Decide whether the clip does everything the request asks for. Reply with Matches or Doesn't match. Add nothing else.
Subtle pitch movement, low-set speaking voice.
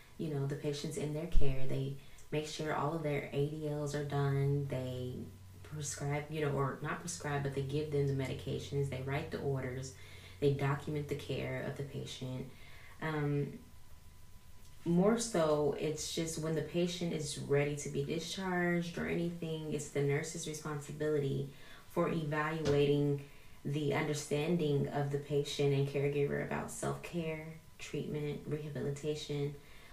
Doesn't match